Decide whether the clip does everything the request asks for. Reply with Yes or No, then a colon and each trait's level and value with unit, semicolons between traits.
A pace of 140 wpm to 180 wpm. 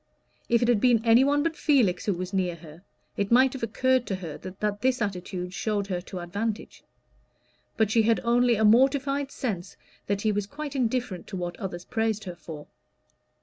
No: average, 190 wpm